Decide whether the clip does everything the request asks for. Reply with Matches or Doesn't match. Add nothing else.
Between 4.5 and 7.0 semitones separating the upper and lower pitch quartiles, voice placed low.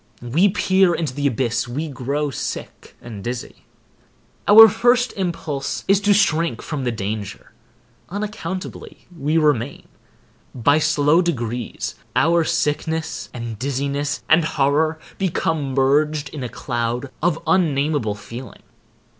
Doesn't match